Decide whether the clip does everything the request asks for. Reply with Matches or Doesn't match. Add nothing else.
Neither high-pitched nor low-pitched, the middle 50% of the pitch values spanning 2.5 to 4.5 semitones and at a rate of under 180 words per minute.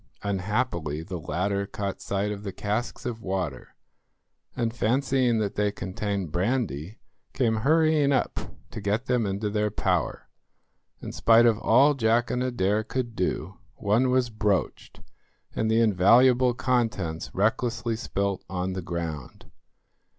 Doesn't match